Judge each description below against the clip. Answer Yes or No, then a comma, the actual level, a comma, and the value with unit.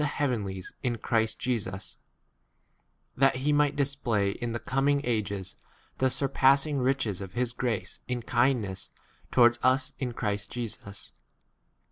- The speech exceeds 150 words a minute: No, slow, 135 wpm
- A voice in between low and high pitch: No, low, 120 Hz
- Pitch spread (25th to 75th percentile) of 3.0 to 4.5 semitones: Yes, average, 4.1 semitones